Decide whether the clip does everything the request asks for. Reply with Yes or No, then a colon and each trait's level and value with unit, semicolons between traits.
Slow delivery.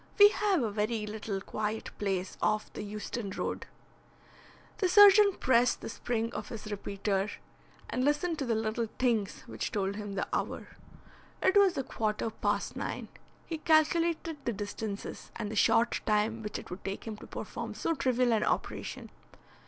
No: average, 170 wpm